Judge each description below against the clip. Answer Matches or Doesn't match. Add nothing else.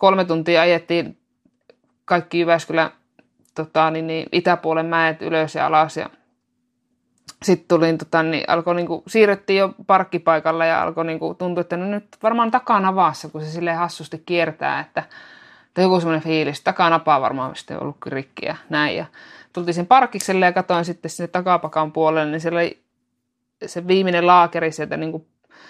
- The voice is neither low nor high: Matches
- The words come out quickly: Matches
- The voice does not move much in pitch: Matches